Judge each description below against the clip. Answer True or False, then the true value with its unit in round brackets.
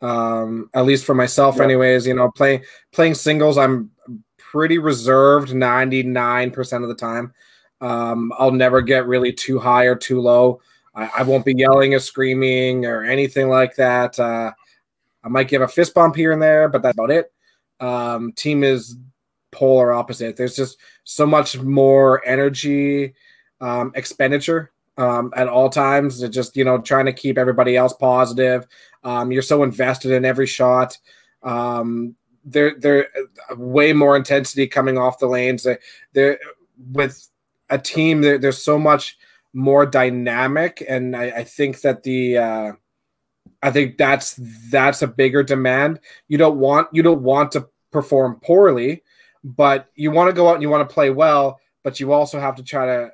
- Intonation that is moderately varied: False (2.1 semitones)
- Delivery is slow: False (170 wpm)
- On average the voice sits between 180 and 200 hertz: False (130 Hz)